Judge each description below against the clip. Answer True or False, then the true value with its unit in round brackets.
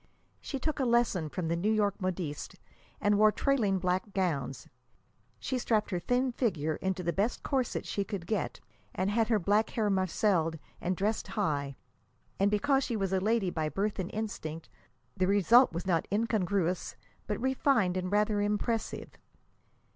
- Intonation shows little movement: False (3.6 semitones)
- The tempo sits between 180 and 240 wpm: False (165 wpm)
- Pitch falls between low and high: False (200 Hz)